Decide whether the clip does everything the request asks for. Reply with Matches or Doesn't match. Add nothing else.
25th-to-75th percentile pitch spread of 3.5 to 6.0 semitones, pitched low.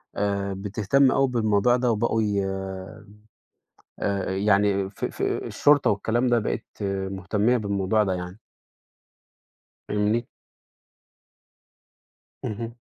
Doesn't match